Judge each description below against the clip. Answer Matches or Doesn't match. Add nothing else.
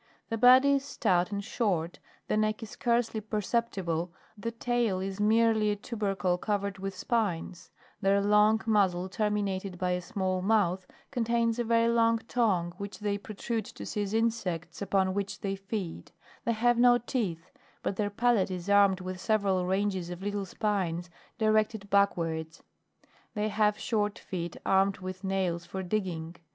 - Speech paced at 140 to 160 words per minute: Matches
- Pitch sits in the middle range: Doesn't match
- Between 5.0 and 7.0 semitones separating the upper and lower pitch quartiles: Doesn't match